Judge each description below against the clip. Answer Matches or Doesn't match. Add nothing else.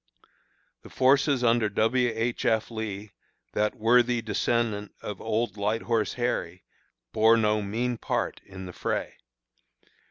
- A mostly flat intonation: Matches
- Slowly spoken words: Matches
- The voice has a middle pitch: Doesn't match